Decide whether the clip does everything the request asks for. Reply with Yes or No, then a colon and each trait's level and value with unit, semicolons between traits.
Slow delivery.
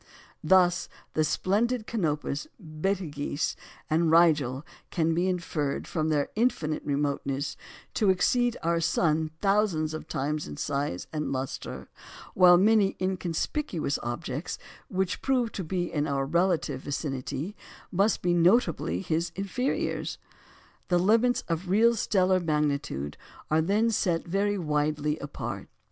Yes: slow, 125 wpm